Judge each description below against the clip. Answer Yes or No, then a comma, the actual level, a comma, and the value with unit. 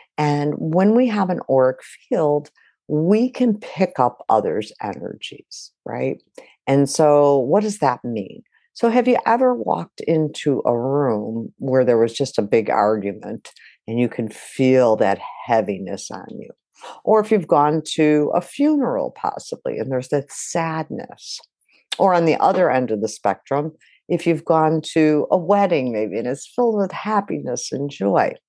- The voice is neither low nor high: Yes, medium, 155 Hz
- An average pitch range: No, wide, 7.6 semitones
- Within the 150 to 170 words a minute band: Yes, average, 160 wpm